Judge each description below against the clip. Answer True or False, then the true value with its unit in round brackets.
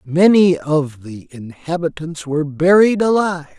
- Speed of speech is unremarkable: False (115 wpm)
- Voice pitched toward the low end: False (165 Hz)